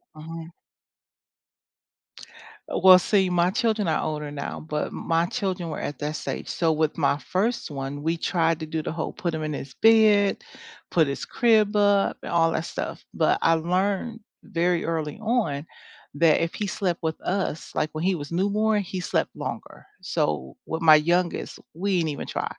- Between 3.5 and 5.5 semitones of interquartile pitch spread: Yes, average, 4.0 semitones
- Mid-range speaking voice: Yes, medium, 170 Hz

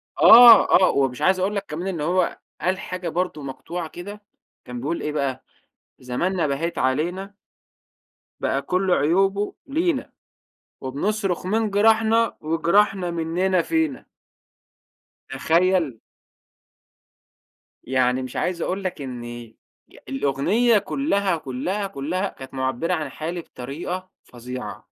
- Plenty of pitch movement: Yes, wide, 6.0 semitones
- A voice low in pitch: No, medium, 175 Hz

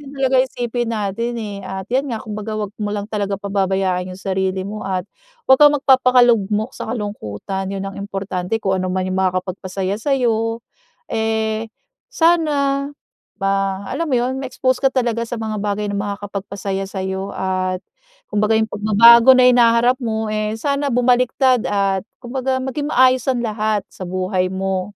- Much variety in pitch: No, average, 4.1 semitones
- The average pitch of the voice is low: No, high, 215 Hz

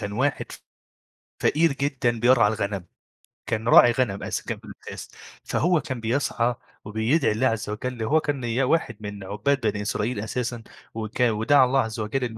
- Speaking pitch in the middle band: No, low, 120 Hz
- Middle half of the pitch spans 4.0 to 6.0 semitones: No, average, 3.5 semitones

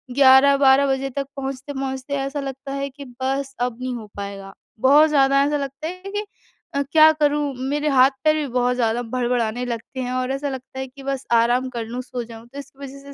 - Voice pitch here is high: Yes, very high, 270 Hz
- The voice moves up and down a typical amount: No, narrow, 2.0 semitones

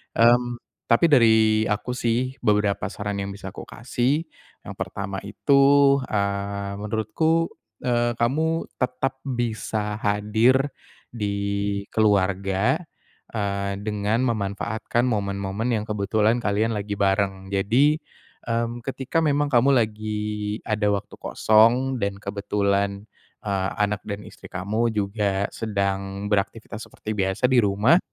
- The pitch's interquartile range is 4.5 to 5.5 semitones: No, average, 3.1 semitones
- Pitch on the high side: No, low, 105 Hz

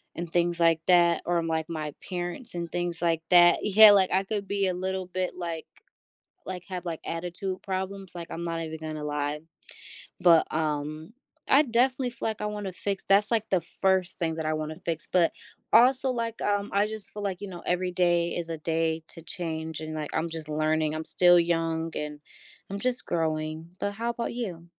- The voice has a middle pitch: Yes, medium, 175 Hz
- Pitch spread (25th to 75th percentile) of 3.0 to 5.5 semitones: Yes, average, 3.3 semitones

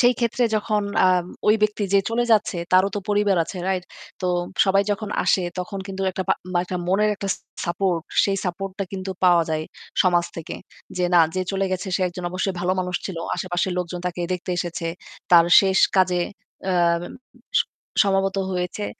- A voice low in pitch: No, medium, 185 Hz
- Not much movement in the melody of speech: Yes, narrow, 1.8 semitones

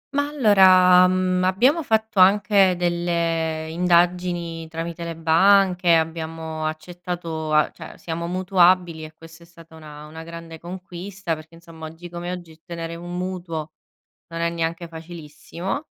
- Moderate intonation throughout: No, narrow, 2.0 semitones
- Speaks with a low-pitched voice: No, medium, 170 Hz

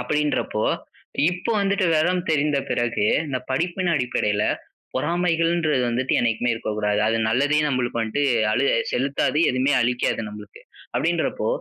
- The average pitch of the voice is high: No, low, 135 Hz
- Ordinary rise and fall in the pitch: No, wide, 5.7 semitones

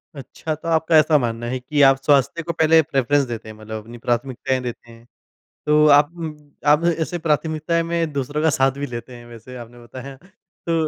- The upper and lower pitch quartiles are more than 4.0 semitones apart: Yes, average, 4.6 semitones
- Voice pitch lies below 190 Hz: Yes, medium, 140 Hz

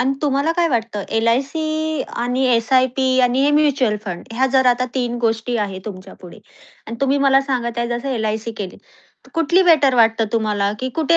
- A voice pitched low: No, high, 245 Hz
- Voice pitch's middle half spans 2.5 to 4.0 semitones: Yes, average, 3.5 semitones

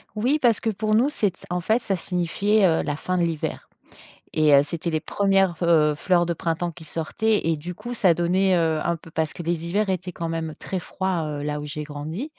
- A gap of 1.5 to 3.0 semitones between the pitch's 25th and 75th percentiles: No, average, 3.4 semitones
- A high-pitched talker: No, medium, 175 Hz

